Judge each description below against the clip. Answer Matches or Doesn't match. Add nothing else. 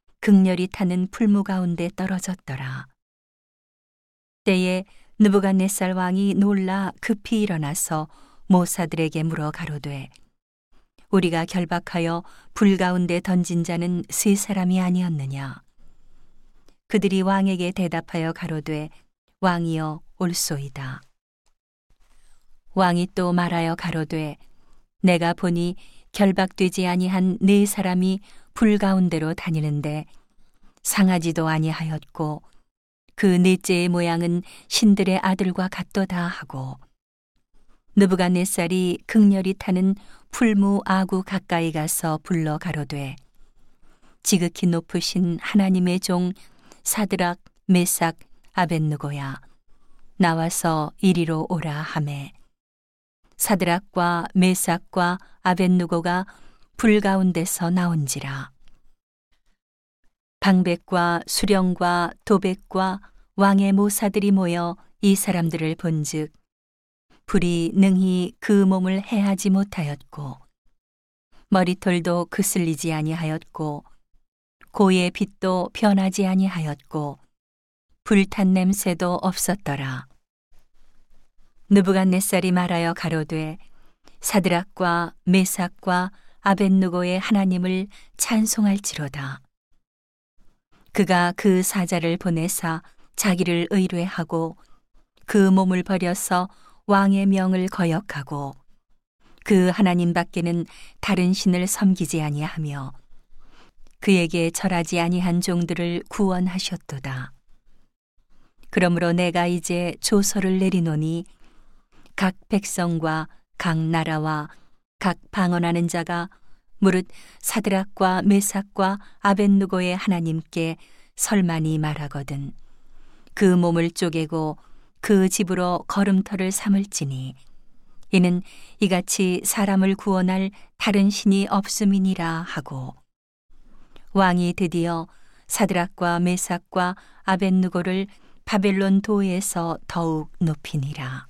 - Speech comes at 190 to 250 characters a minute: Matches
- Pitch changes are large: Doesn't match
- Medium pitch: Matches